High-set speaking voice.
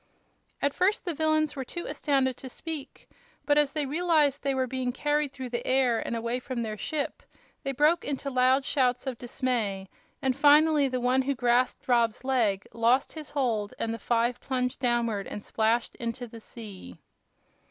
Yes: very high, 255 Hz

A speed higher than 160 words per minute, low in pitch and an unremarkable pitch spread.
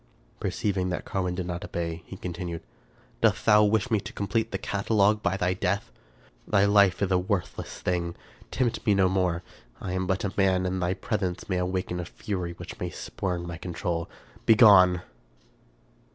No: average, 180 wpm; very low, 95 Hz; narrow, 2.1 semitones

